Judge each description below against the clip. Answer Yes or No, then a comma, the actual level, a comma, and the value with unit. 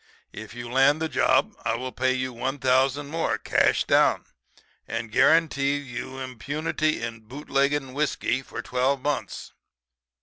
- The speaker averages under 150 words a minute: Yes, average, 140 wpm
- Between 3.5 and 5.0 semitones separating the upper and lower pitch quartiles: No, narrow, 2.4 semitones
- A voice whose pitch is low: Yes, low, 130 Hz